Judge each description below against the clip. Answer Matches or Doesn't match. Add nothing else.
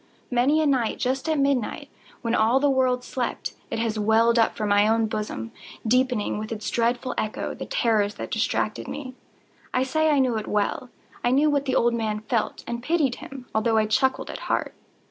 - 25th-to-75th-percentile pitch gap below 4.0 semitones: Matches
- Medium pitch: Doesn't match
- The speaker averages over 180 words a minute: Matches